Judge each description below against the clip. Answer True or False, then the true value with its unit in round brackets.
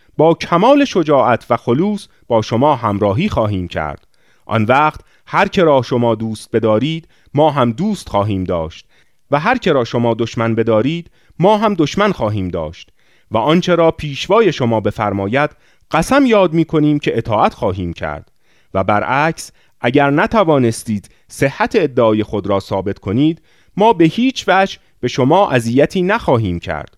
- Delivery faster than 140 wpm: True (150 wpm)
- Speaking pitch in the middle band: False (125 Hz)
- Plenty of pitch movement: True (7.4 semitones)